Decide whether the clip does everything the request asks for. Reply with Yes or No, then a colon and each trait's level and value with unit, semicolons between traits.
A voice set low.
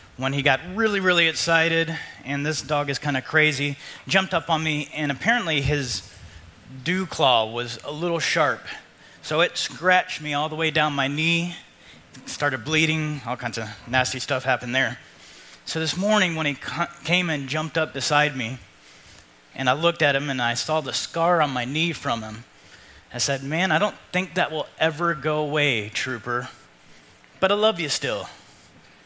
No: medium, 150 Hz